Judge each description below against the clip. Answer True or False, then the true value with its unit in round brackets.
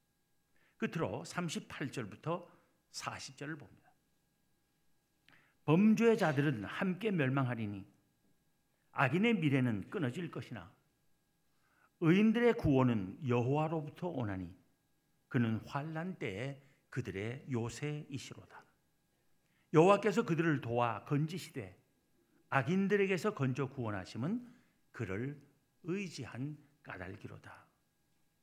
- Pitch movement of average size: True (4.6 semitones)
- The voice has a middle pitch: True (145 Hz)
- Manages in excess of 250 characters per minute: False (215 characters per minute)